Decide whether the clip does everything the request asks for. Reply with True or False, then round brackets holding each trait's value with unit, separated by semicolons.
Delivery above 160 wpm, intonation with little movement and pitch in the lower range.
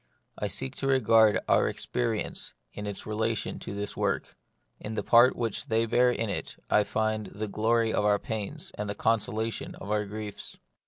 True (190 wpm; 1.6 semitones; 110 Hz)